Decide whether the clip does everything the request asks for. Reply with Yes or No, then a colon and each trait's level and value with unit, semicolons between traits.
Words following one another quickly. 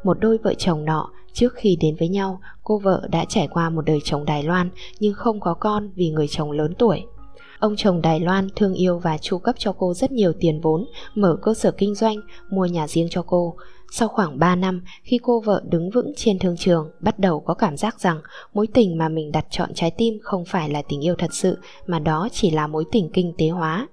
No: average, 240 wpm